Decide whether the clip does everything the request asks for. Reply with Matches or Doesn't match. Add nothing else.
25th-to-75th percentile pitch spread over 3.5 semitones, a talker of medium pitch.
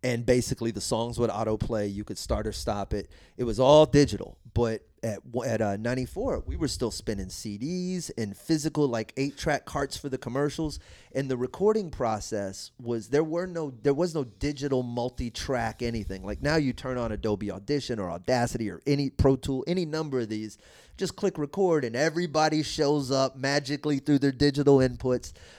Doesn't match